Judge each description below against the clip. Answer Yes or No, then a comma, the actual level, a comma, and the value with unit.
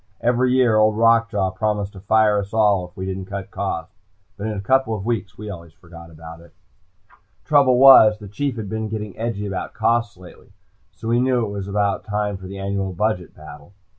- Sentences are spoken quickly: Yes, fast, 210 wpm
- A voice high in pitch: No, low, 105 Hz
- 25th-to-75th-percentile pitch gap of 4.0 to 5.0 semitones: No, average, 2.9 semitones